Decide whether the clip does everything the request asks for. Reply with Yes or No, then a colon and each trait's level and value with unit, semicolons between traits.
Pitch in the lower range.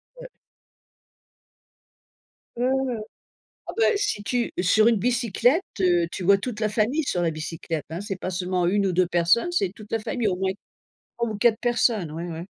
No: high, 205 Hz